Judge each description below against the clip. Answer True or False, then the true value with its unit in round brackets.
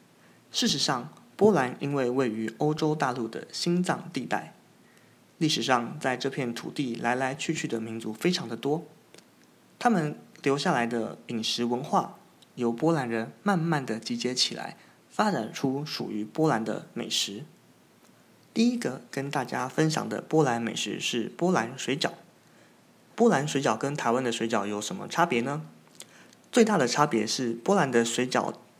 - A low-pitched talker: True (130 Hz)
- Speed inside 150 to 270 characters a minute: True (235 characters per minute)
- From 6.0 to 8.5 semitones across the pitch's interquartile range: False (5.1 semitones)